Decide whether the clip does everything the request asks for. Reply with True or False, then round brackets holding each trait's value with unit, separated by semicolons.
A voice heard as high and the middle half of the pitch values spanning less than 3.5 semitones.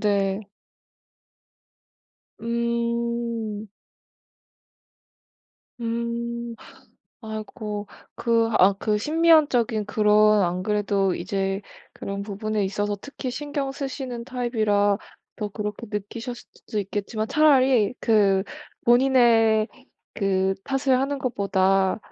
True (220 Hz; 2.7 semitones)